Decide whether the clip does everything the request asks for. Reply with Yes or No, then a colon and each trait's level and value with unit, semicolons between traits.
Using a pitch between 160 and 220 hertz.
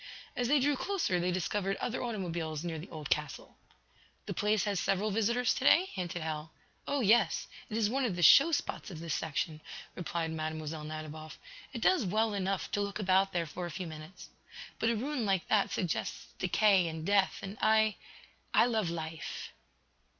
Yes: high, 190 Hz